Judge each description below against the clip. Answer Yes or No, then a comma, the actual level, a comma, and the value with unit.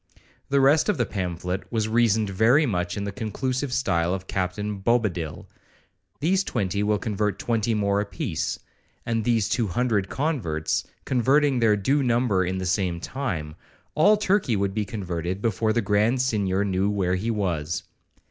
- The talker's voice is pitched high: No, low, 105 Hz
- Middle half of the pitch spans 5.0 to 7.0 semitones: No, average, 4.5 semitones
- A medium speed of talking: Yes, average, 160 wpm